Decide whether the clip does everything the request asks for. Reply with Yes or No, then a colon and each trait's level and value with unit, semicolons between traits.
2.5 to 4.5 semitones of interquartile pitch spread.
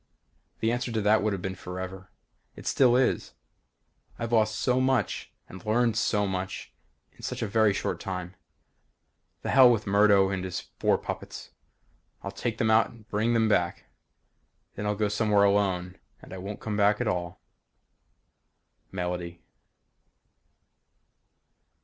Yes: average, 2.9 semitones